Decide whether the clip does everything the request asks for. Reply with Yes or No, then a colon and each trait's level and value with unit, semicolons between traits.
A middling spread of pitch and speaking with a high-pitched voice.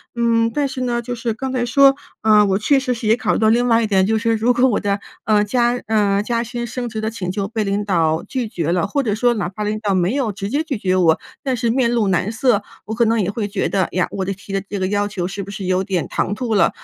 Yes: average, 3.3 semitones; high, 215 Hz